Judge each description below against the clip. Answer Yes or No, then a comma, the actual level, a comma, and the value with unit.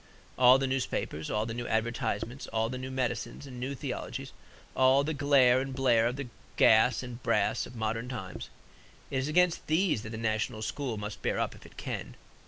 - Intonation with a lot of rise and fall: No, average, 3.0 semitones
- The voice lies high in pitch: No, low, 125 Hz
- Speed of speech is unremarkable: Yes, average, 195 wpm